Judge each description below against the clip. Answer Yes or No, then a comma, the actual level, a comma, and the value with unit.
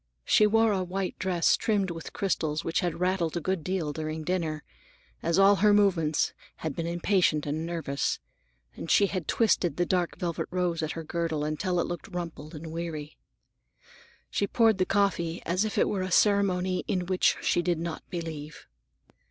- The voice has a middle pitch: Yes, medium, 175 Hz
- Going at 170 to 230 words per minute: Yes, average, 180 wpm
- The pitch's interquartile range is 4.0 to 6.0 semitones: No, average, 2.8 semitones